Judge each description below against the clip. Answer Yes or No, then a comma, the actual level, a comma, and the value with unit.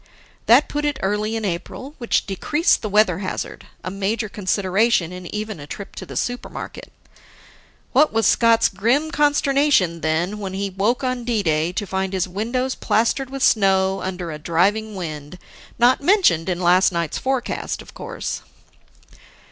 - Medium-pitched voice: No, high, 205 Hz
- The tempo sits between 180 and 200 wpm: No, average, 160 wpm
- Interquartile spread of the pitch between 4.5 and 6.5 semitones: Yes, average, 4.9 semitones